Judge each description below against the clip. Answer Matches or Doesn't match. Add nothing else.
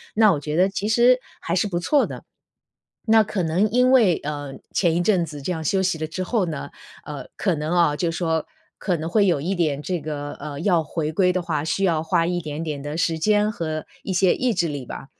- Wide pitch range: Doesn't match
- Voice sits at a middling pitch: Matches